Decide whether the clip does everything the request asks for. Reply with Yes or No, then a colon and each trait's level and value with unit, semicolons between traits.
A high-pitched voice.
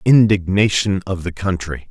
No: very low, 95 Hz